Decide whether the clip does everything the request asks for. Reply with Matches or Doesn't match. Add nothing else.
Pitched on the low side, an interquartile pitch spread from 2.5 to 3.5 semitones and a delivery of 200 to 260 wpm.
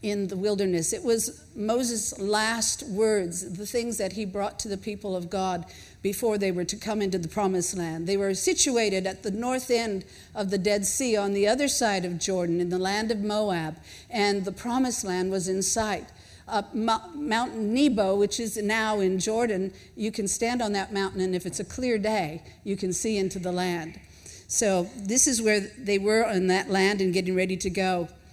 Doesn't match